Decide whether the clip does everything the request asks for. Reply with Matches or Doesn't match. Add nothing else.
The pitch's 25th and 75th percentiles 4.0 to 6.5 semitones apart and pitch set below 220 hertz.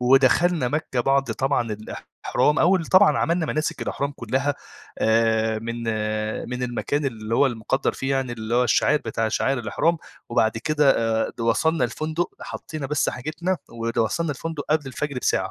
Matches